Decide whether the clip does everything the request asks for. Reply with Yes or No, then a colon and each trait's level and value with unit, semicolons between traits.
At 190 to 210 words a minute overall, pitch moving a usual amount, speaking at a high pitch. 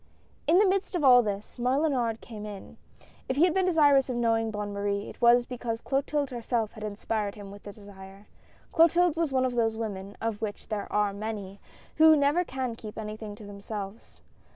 Yes: average, 200 wpm; average, 4.6 semitones; high, 225 Hz